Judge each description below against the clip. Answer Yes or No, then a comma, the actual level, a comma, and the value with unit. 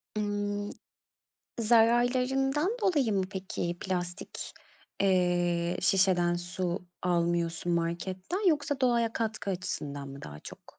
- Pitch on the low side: No, high, 190 Hz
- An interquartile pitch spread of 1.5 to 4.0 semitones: No, average, 5.2 semitones